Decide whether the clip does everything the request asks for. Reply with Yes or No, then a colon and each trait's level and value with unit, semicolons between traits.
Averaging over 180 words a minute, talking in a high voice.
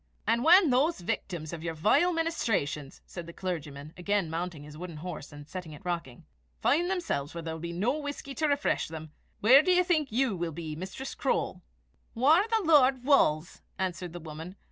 No: average, 190 wpm; medium, 180 Hz